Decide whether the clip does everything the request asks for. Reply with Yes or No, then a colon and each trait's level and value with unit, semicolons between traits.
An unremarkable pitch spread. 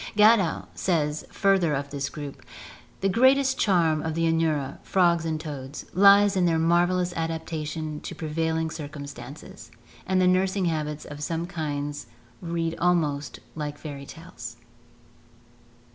Yes: average, 3.1 semitones